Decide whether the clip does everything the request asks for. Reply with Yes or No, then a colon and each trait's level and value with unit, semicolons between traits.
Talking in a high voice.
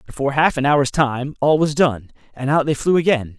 No: medium, 140 Hz